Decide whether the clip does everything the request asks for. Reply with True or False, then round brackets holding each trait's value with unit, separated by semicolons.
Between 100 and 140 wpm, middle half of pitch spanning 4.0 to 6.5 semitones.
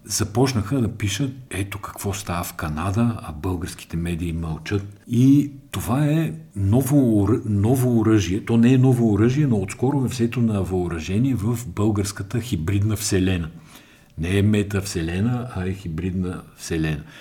True (135 wpm; 4.5 semitones)